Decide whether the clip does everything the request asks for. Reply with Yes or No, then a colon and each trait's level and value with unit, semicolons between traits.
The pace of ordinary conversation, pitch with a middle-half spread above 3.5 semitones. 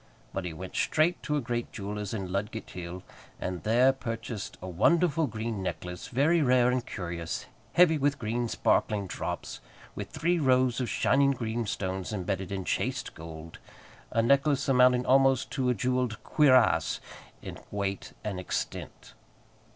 Yes: average, 150 wpm; wide, 5.5 semitones